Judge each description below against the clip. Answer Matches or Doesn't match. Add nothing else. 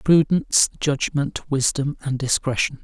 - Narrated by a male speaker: Matches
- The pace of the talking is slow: Matches